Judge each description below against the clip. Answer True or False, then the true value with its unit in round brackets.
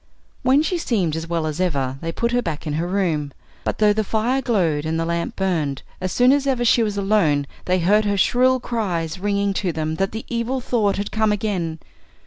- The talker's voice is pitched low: False (195 Hz)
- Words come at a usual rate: False (220 wpm)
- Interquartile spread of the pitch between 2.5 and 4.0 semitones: False (5.6 semitones)